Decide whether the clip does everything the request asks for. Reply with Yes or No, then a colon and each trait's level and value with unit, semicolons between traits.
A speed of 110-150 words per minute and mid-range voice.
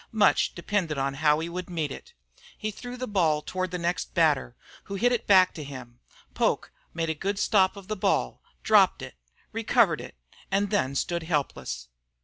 No: average, 185 wpm; medium, 175 Hz